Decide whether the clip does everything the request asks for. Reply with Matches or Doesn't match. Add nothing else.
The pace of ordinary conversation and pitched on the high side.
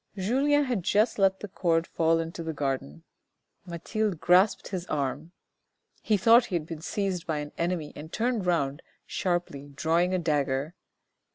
Doesn't match